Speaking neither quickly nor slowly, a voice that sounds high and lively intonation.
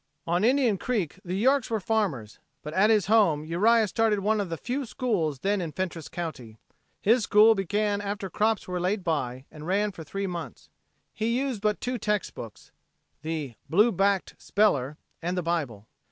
No: average, 180 wpm; high, 195 Hz; average, 4.8 semitones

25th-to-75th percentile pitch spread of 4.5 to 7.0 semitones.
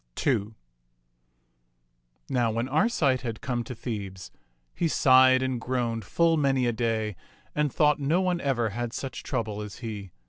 No: average, 3.6 semitones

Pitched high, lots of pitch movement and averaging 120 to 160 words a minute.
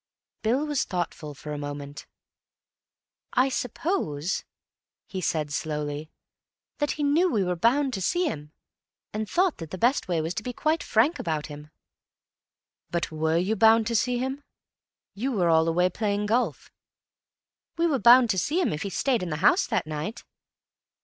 No: high, 200 Hz; wide, 8.3 semitones; average, 170 wpm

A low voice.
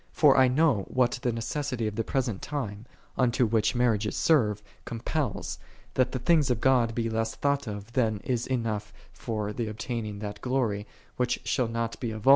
Yes: low, 115 Hz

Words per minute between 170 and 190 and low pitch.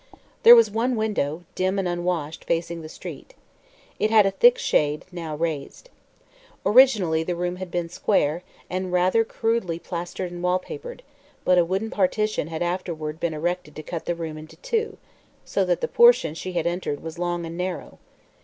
No: average, 175 wpm; medium, 180 Hz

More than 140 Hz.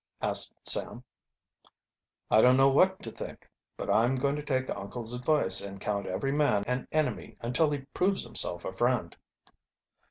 No: low, 125 Hz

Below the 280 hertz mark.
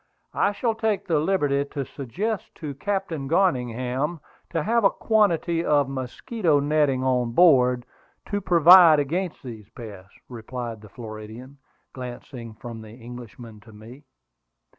Yes: low, 135 Hz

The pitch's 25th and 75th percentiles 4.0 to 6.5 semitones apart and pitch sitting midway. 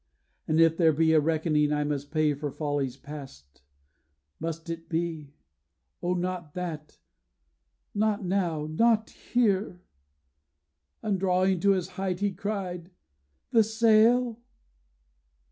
Yes: average, 4.3 semitones; medium, 170 Hz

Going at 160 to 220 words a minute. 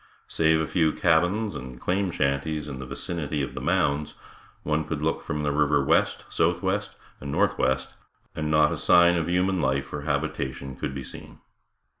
Yes: average, 175 wpm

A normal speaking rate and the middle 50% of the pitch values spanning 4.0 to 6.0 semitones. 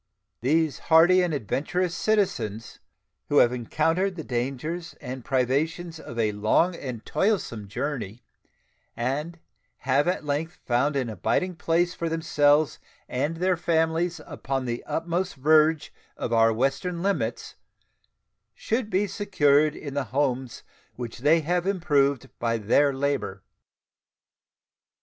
No: slow, 125 wpm; average, 5.0 semitones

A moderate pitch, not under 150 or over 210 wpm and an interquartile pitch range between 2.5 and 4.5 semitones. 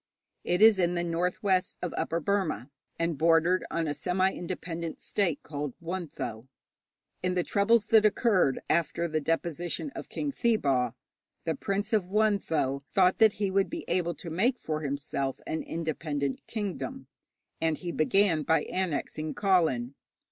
Yes: medium, 170 Hz; average, 155 wpm; average, 4.1 semitones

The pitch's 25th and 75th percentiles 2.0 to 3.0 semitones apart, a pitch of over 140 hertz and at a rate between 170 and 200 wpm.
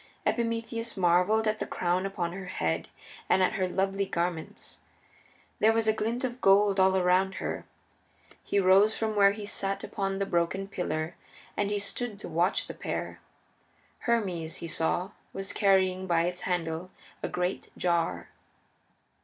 No: average, 2.7 semitones; high, 190 Hz; average, 155 wpm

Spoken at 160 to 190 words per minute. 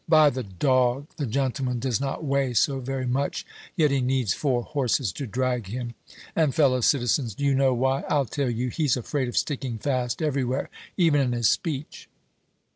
Yes: average, 185 wpm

